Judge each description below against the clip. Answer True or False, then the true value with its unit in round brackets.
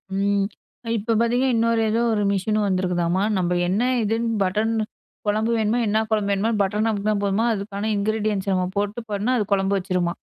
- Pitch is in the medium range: False (205 Hz)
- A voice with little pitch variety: True (2.1 semitones)